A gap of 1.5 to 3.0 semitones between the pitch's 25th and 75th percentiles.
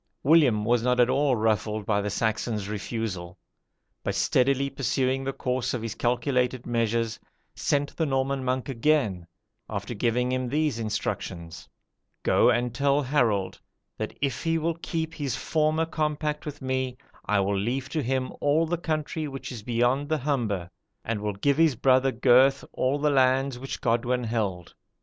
No: average, 3.8 semitones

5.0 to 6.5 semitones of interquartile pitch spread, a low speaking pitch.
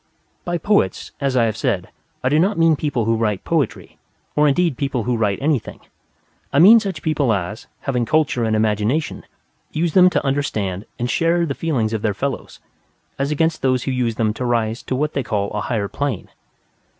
Yes: wide, 5.6 semitones; low, 130 Hz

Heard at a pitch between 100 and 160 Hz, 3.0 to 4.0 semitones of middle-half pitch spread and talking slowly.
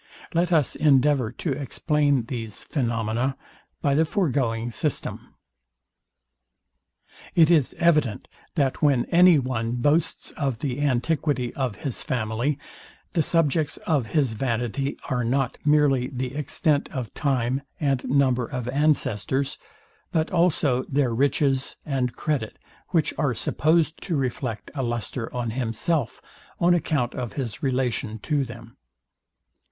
Yes: low, 135 Hz; average, 3.6 semitones; slow, 125 wpm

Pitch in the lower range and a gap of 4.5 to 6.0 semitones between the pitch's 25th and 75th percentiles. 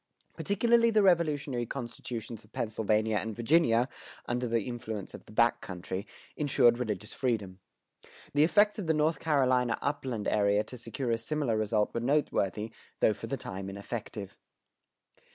Yes: low, 120 Hz; average, 5.1 semitones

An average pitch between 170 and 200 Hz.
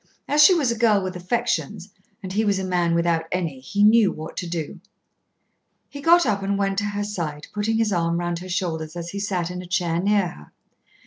Yes: medium, 185 Hz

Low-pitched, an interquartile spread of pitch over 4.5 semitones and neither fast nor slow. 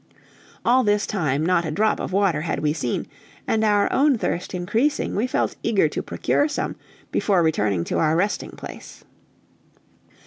No: high, 190 Hz; wide, 5.4 semitones; average, 165 wpm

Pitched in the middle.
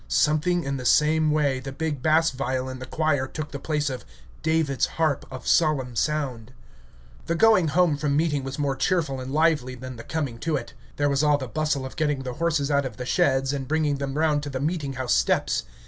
Yes: medium, 145 Hz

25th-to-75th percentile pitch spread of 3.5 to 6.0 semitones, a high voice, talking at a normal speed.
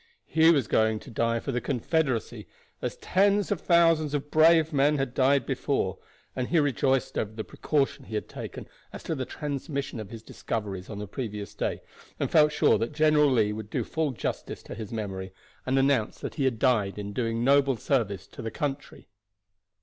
No: average, 5.2 semitones; low, 130 Hz; average, 195 wpm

